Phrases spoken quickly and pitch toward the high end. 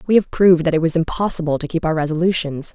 No: fast, 240 wpm; medium, 165 Hz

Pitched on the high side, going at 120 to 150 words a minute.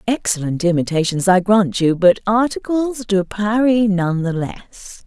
Yes: high, 200 Hz; average, 140 wpm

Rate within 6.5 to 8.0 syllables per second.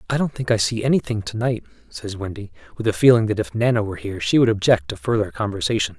Yes: 6.8 syllables/s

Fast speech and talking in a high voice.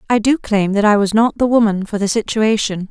Yes: fast, 250 wpm; high, 215 Hz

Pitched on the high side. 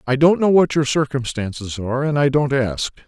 No: low, 135 Hz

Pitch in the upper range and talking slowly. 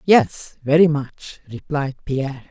No: medium, 140 Hz; slow, 120 wpm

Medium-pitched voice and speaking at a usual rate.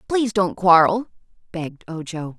No: medium, 180 Hz; slow, 125 wpm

